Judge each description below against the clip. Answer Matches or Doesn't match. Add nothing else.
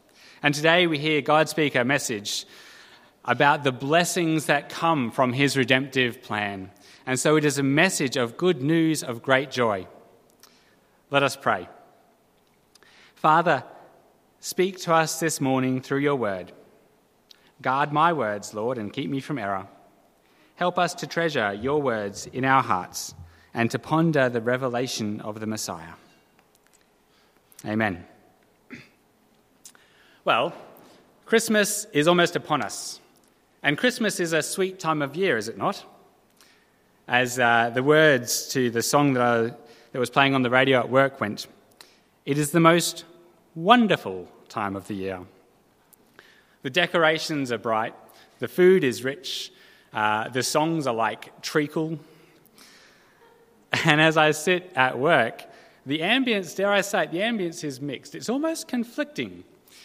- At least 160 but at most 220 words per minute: Doesn't match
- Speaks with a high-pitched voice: Doesn't match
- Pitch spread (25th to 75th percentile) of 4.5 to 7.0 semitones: Matches